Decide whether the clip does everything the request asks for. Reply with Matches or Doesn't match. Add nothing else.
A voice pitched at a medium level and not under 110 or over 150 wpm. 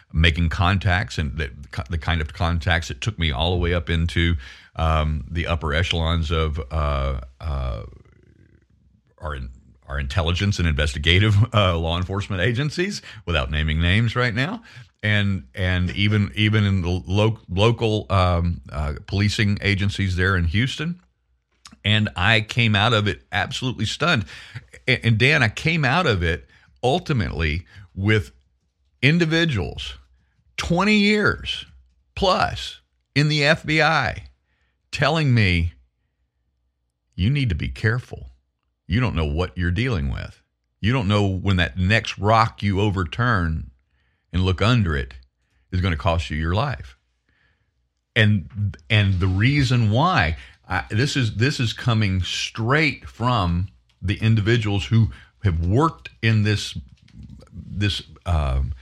Doesn't match